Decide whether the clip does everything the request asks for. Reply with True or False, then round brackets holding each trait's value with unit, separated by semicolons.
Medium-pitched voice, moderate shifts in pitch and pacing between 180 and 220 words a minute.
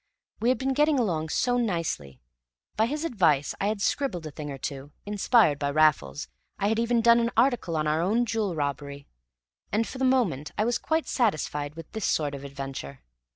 False (180 Hz; 8.4 semitones; 200 wpm)